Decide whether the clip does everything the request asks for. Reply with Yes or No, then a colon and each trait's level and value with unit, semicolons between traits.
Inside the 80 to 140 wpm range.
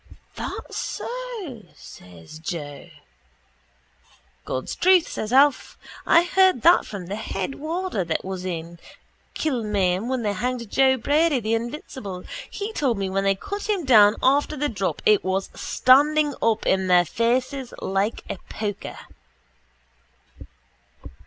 Yes: slow, 135 wpm